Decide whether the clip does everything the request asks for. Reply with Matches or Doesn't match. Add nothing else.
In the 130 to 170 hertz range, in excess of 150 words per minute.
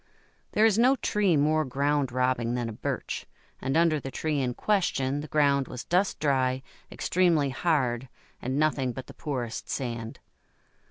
Matches